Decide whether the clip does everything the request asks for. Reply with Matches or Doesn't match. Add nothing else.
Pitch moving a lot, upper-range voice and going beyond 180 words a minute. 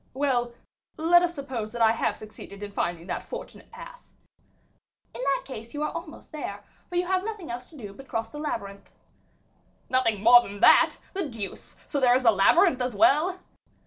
Matches